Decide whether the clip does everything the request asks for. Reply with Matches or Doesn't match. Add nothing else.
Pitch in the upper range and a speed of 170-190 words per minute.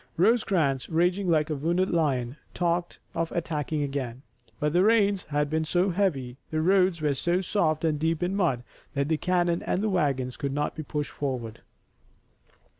Doesn't match